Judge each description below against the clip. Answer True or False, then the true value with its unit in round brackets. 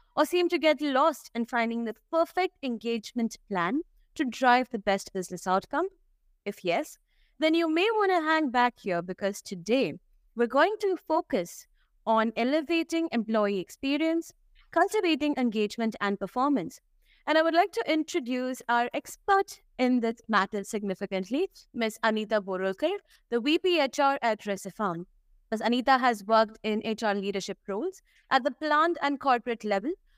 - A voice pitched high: True (250 Hz)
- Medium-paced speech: True (150 wpm)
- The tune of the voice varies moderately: False (6.7 semitones)